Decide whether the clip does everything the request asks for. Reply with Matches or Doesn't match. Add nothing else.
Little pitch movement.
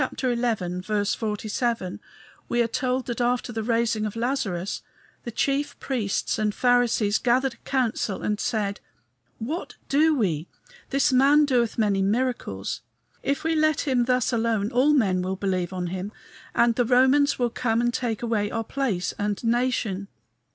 Doesn't match